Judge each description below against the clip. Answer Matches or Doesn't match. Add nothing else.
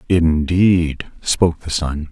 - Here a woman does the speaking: Doesn't match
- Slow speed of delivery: Matches